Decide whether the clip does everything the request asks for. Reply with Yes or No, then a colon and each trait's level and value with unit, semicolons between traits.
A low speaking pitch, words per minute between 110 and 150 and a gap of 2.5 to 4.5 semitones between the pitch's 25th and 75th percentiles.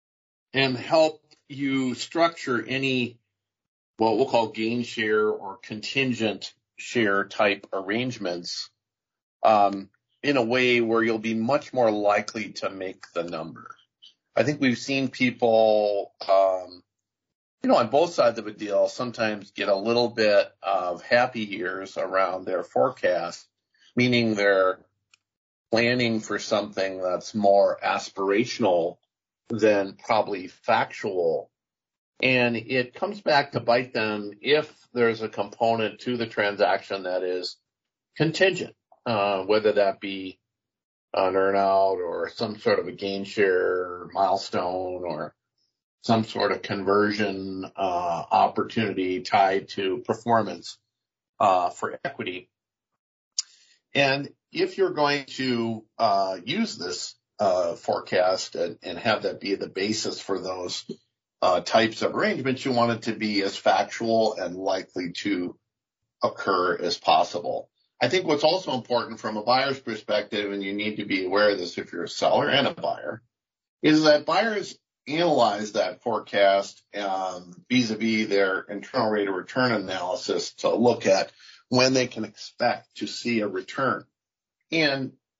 Yes: low, 110 Hz; slow, 135 wpm; average, 4.2 semitones